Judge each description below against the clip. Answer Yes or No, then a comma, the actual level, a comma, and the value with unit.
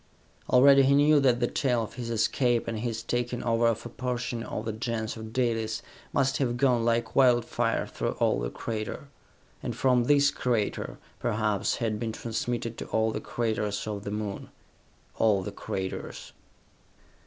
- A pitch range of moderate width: No, narrow, 2.1 semitones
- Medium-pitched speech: No, low, 115 Hz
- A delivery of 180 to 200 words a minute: No, average, 165 wpm